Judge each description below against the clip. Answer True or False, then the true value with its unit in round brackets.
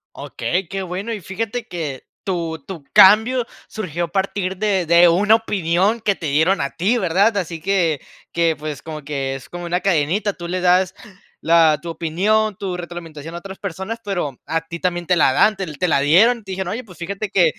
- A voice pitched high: False (180 Hz)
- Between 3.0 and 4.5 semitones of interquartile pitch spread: True (3.4 semitones)